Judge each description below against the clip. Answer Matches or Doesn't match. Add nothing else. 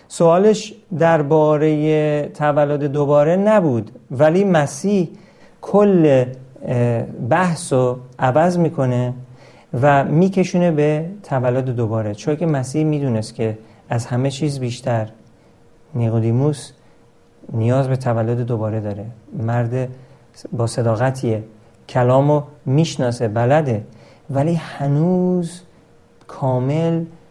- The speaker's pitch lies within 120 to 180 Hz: Matches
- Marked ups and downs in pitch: Doesn't match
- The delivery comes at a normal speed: Doesn't match